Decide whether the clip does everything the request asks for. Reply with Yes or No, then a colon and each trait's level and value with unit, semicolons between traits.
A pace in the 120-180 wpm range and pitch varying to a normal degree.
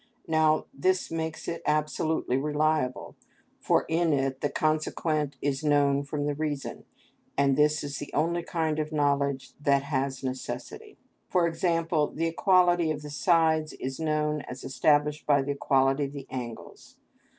No: average, 150 wpm; narrow, 2.1 semitones